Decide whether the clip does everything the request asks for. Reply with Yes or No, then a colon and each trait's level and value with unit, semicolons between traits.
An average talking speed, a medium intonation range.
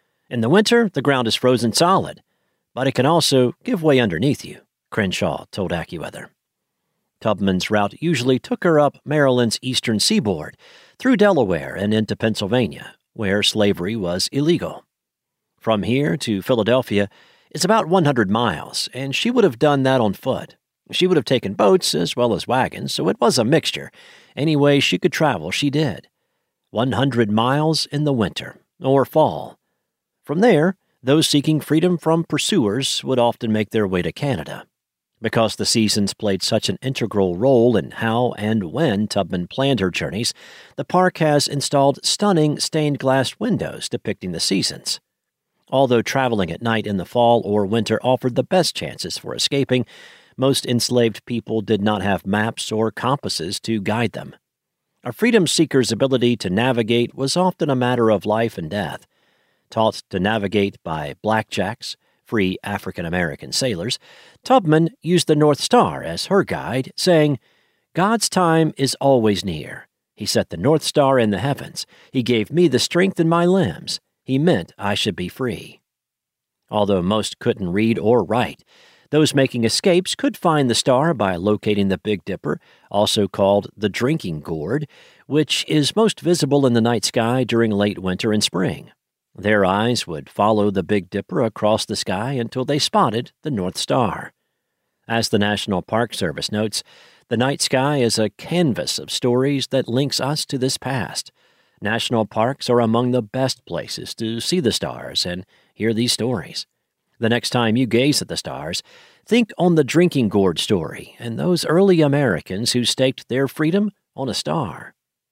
No: average, 165 wpm; wide, 5.7 semitones